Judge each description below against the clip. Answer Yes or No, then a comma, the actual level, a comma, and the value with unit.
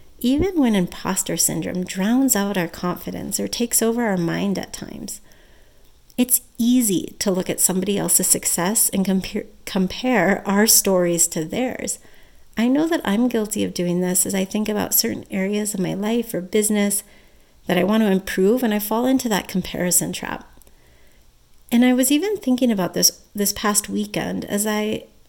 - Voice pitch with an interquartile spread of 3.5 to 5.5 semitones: Yes, average, 4.4 semitones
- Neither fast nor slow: Yes, average, 175 wpm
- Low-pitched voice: No, high, 205 Hz